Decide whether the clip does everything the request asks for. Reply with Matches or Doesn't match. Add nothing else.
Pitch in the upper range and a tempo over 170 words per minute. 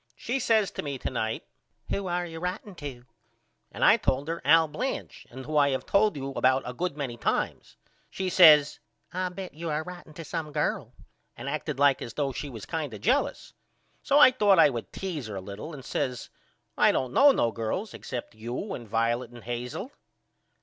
Doesn't match